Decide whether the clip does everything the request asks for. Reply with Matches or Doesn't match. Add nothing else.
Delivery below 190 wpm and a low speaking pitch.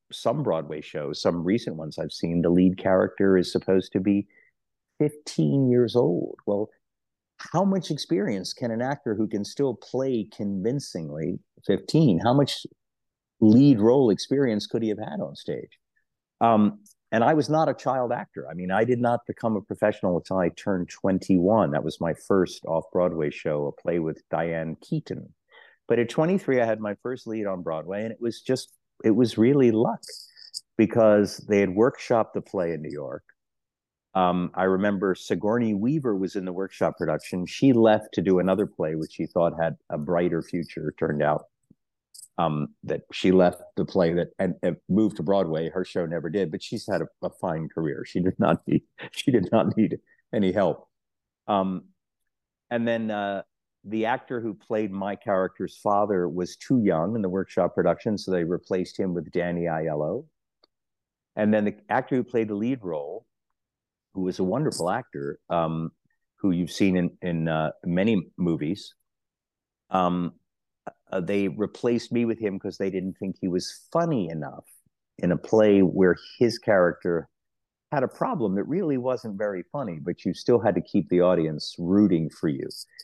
Matches